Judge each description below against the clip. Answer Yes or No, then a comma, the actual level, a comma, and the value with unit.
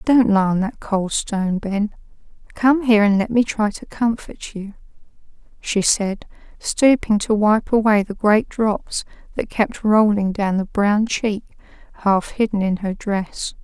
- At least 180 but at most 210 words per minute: No, average, 165 wpm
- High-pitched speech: Yes, high, 210 Hz